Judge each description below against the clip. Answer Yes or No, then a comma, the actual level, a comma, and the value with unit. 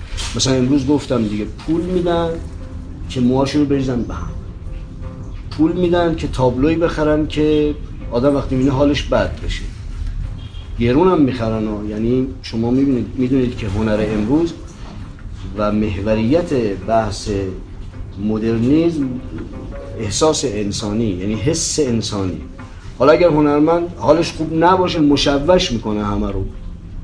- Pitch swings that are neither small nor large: No, wide, 6.9 semitones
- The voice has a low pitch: Yes, low, 110 Hz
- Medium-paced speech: Yes, average, 120 wpm